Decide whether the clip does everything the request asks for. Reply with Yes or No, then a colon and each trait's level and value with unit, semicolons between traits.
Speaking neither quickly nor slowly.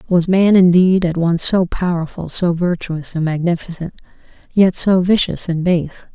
Yes: average, 155 wpm